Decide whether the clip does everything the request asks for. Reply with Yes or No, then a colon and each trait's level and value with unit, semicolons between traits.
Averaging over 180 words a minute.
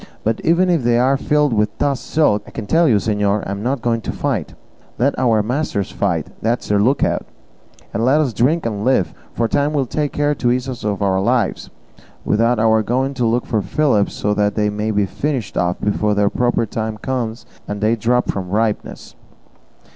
Yes: fast, 205 wpm